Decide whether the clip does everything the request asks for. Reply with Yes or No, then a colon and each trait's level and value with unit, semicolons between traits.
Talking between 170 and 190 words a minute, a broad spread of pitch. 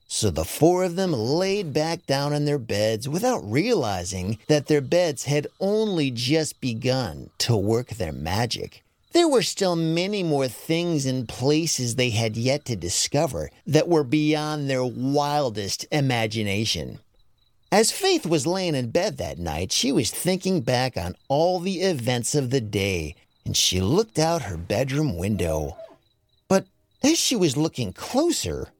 No: average, 155 wpm; wide, 7.1 semitones